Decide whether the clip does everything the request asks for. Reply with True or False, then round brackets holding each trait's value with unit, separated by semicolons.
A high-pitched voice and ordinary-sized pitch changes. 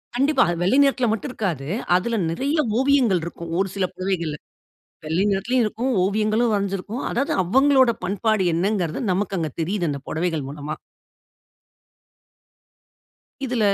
False (200 Hz; 5.8 semitones)